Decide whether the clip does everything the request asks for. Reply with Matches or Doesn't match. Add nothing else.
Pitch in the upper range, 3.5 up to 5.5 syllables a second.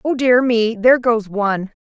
Matches